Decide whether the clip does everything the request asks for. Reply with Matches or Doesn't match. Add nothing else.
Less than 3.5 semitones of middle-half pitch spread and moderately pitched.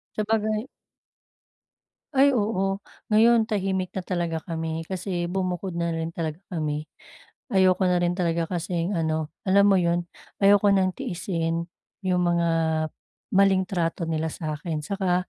Matches